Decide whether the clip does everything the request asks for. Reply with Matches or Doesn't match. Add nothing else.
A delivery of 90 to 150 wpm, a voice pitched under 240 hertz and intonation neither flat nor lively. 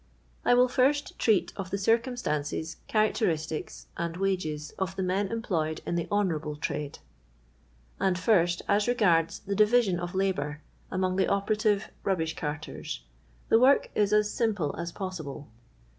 Matches